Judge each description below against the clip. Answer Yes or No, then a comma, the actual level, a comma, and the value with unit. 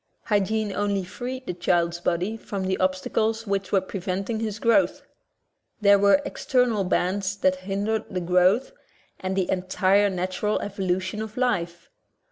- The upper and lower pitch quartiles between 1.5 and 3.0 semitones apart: Yes, narrow, 2.6 semitones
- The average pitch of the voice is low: No, high, 195 Hz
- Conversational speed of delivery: Yes, average, 145 wpm